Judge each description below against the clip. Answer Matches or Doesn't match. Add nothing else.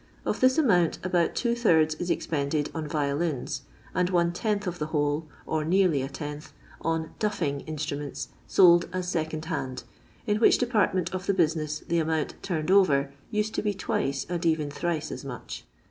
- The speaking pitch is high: Doesn't match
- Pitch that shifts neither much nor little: Matches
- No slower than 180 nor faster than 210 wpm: Matches